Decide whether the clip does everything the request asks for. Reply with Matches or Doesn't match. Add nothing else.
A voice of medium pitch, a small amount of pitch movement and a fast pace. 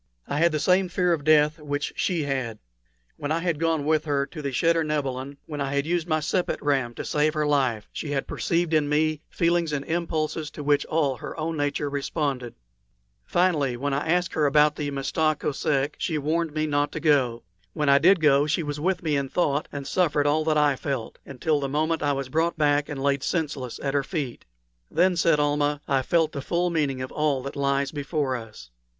Matches